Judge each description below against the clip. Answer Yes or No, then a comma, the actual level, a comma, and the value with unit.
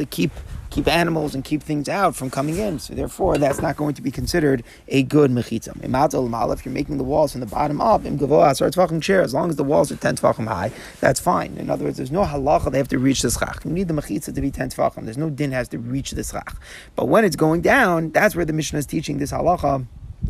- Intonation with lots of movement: No, average, 3.2 semitones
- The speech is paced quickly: Yes, fast, 250 wpm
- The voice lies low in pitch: No, medium, 145 Hz